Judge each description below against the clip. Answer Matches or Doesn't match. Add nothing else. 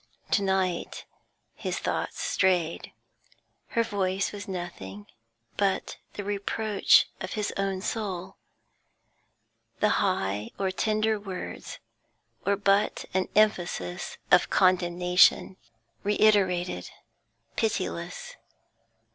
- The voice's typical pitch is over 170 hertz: Matches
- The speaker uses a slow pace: Matches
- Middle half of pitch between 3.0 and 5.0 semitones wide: Doesn't match